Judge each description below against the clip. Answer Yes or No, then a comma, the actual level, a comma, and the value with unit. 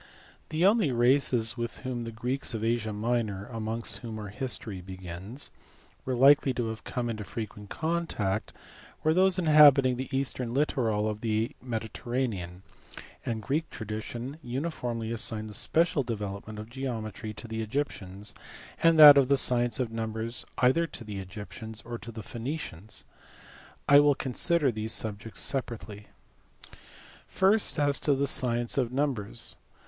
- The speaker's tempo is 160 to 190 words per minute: No, average, 145 wpm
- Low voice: Yes, low, 120 Hz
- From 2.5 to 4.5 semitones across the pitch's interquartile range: Yes, average, 3.9 semitones